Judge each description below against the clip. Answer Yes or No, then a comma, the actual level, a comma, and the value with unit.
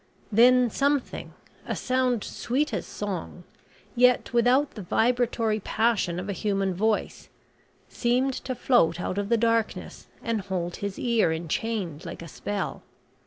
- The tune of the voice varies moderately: Yes, average, 4.2 semitones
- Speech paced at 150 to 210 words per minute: No, average, 140 wpm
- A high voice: Yes, high, 225 Hz